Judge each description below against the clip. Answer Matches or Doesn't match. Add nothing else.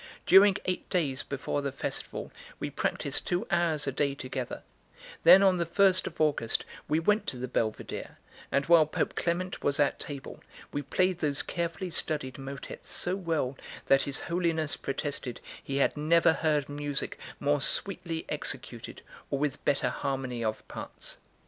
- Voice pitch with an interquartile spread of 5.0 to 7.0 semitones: Doesn't match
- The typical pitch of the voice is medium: Matches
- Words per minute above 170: Doesn't match